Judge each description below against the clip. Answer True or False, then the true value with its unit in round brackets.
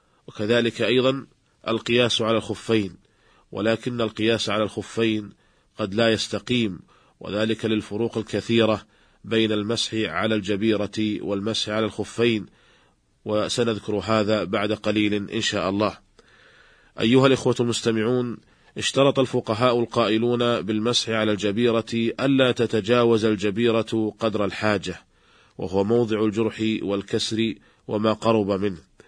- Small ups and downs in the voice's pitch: True (1.6 semitones)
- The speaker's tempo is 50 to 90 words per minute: False (105 wpm)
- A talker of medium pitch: False (110 Hz)